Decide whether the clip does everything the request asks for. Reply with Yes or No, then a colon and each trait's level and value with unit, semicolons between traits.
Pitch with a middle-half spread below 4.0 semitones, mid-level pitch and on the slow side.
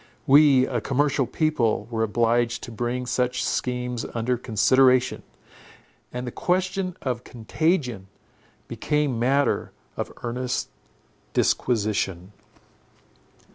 No: average, 2.7 semitones; low, 125 Hz; slow, 95 wpm